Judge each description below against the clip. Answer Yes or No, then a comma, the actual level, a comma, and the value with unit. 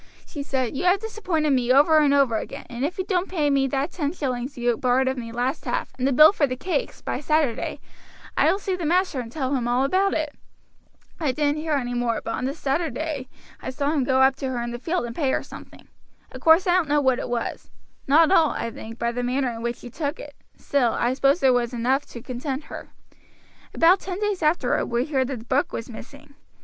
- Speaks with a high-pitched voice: Yes, very high, 275 Hz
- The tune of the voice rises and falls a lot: No, average, 4.1 semitones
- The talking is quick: Yes, fast, 240 wpm